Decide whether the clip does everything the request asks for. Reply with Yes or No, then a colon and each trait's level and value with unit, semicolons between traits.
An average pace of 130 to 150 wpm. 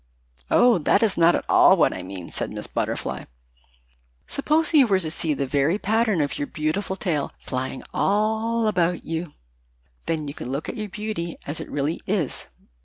No: average, 180 wpm